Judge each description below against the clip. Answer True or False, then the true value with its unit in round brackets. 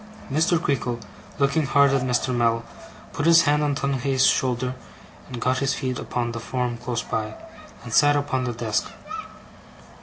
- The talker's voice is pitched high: False (130 Hz)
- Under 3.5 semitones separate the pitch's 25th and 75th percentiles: True (2.8 semitones)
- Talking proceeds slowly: False (160 wpm)